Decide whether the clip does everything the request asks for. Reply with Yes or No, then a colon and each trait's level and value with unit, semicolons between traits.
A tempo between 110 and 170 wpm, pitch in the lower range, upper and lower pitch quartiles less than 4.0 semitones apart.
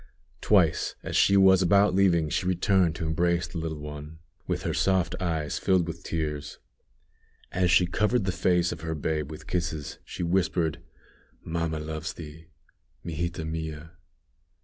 Yes: average, 150 wpm; very low, 85 Hz; narrow, 2.4 semitones